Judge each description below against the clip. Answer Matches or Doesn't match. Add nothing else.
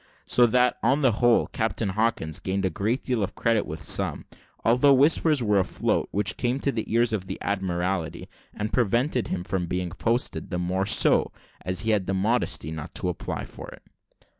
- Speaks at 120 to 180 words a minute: Doesn't match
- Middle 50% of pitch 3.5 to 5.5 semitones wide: Matches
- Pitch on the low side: Matches